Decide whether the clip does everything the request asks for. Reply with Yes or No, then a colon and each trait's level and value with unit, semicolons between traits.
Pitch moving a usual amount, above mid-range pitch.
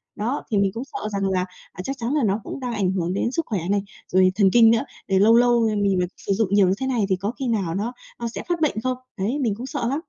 Yes: average, 3.9 semitones; high, 215 Hz